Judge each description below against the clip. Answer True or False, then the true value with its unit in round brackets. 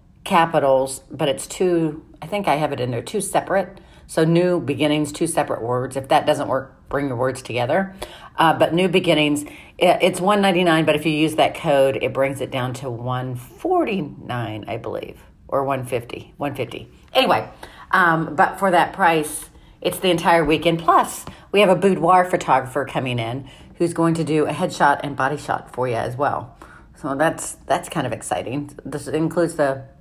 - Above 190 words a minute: False (180 wpm)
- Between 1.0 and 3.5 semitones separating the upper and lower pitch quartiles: False (4.2 semitones)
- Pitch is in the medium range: True (155 Hz)